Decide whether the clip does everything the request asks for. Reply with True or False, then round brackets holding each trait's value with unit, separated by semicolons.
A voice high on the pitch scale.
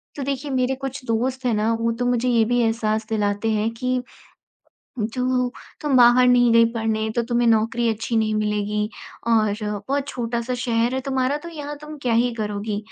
True (235 Hz)